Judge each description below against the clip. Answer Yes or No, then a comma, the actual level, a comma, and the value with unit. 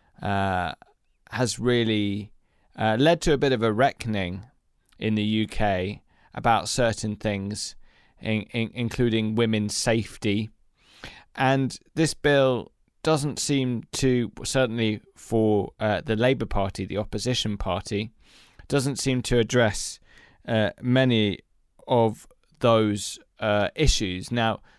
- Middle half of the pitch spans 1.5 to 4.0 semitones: Yes, average, 3.3 semitones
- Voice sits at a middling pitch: No, low, 110 Hz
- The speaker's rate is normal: No, slow, 115 wpm